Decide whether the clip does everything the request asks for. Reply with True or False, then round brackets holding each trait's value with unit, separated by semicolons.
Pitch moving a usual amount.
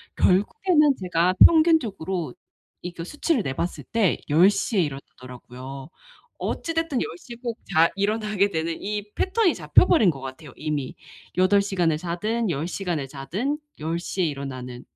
False (6.6 semitones)